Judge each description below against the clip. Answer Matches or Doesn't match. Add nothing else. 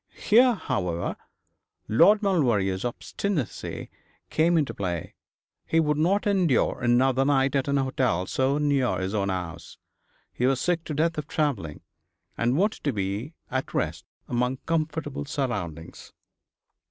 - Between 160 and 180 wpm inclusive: Doesn't match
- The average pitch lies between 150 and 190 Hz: Doesn't match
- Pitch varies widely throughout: Matches